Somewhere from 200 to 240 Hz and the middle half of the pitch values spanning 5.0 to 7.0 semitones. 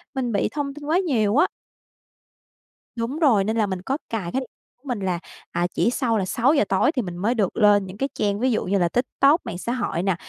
Yes: high, 230 Hz; wide, 5.5 semitones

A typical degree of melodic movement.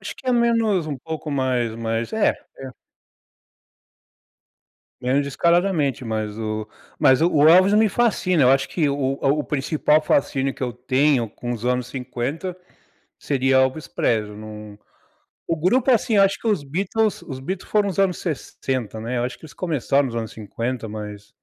No: wide, 6.4 semitones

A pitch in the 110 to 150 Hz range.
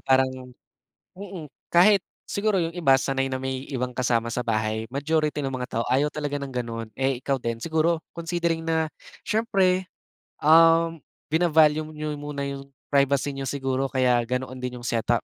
Yes: medium, 140 Hz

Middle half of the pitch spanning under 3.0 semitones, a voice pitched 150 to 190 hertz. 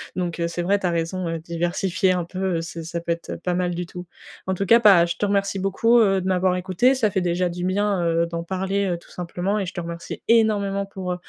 Yes: narrow, 2.4 semitones; medium, 185 Hz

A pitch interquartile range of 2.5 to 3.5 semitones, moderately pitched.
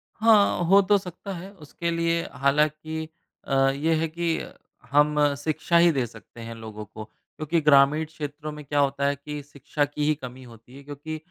Yes: average, 2.8 semitones; medium, 150 Hz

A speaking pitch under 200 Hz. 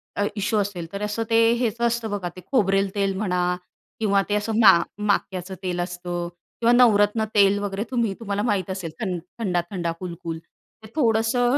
No: high, 205 Hz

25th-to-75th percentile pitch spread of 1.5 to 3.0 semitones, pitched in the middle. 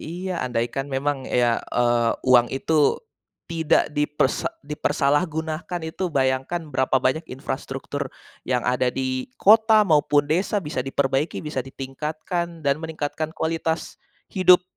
No: average, 3.6 semitones; medium, 145 Hz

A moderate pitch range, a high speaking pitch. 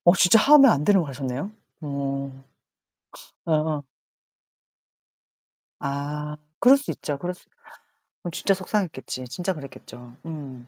No: average, 4.9 semitones; medium, 150 Hz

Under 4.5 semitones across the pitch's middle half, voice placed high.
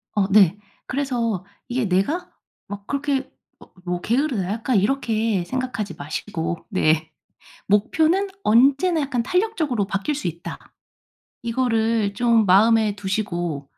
No: average, 5.3 semitones; high, 225 Hz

